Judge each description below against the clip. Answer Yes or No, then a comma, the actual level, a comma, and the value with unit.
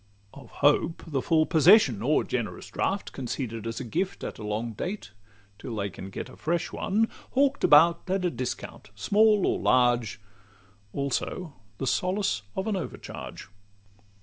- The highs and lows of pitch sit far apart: Yes, wide, 8.2 semitones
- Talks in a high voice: No, medium, 140 Hz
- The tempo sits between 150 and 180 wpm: Yes, average, 155 wpm